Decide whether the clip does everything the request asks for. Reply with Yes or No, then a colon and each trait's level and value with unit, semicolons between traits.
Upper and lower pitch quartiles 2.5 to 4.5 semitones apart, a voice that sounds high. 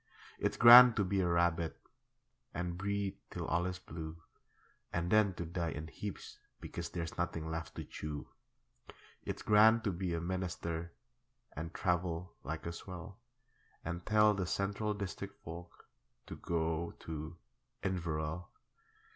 No: average, 3.0 semitones; very low, 85 Hz